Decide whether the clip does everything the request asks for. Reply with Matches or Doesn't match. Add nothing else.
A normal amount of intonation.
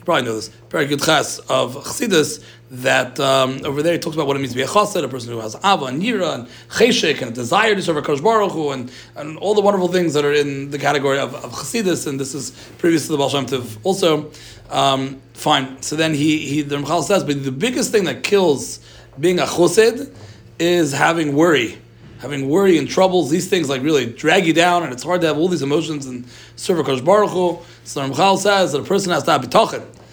Matches